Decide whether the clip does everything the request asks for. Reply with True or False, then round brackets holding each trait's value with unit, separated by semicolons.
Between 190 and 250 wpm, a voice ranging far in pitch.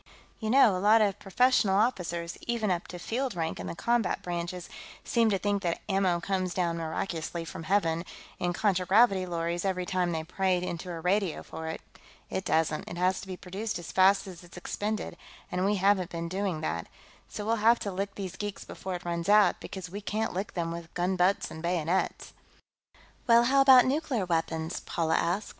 False (195 wpm; 3.1 semitones)